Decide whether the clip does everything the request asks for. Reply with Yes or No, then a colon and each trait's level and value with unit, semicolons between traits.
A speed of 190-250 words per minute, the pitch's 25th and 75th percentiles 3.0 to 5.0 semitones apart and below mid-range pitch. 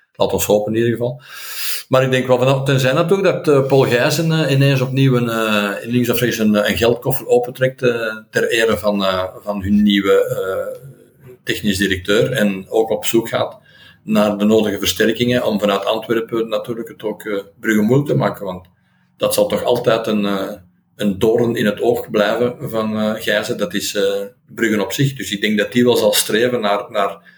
Yes: fast, 200 wpm; average, 3.6 semitones; low, 115 Hz